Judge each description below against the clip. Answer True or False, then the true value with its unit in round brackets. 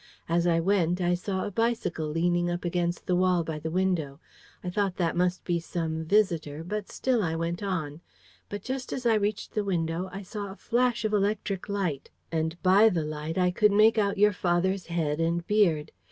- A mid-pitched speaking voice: True (180 Hz)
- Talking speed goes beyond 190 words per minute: True (200 wpm)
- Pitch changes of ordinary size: True (3.5 semitones)